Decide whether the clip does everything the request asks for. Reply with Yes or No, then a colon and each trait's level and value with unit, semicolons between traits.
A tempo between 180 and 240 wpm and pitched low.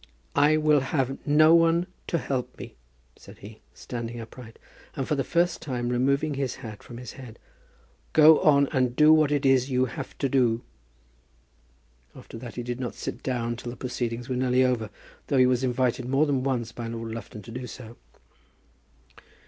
Yes: average, 185 wpm; low, 130 Hz